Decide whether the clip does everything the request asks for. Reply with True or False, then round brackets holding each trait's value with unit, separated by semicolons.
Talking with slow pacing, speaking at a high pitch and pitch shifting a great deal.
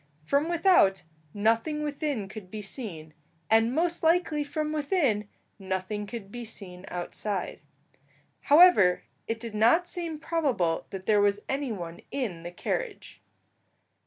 True (130 wpm; 225 Hz; 7.7 semitones)